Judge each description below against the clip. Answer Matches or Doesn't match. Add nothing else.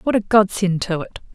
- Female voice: Matches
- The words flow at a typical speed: Doesn't match